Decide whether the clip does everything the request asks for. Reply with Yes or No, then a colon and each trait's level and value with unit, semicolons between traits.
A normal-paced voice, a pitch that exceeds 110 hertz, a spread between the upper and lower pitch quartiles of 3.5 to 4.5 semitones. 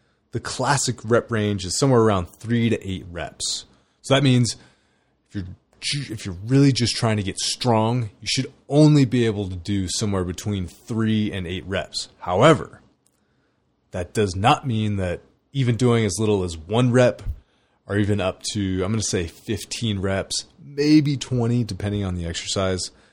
No: average, 170 wpm; low, 105 Hz; average, 4.0 semitones